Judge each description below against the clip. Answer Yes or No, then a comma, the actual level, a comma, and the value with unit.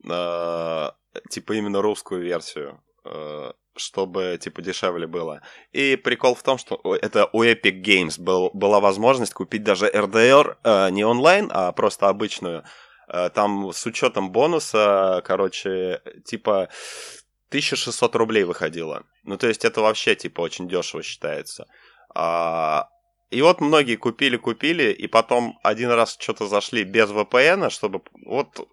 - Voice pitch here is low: Yes, low, 110 Hz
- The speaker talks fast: No, average, 125 wpm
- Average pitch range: Yes, average, 5.0 semitones